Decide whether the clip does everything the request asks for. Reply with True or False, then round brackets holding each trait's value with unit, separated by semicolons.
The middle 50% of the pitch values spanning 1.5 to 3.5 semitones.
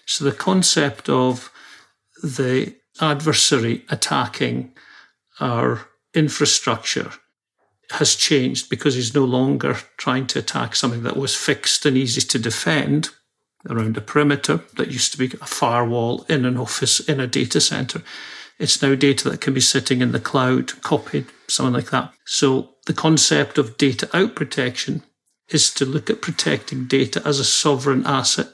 True (2.7 semitones)